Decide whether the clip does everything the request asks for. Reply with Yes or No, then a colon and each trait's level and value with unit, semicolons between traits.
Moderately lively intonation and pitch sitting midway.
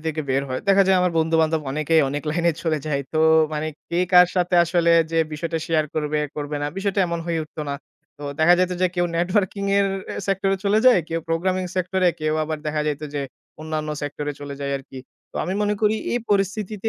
Yes: average, 3.5 semitones; medium, 165 Hz